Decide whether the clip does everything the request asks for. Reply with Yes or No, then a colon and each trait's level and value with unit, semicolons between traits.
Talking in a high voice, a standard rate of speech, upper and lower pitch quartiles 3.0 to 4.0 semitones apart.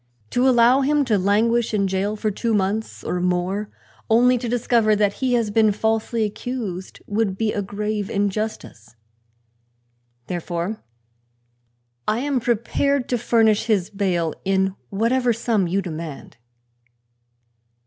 No: high, 215 Hz; slow, 130 wpm; average, 3.3 semitones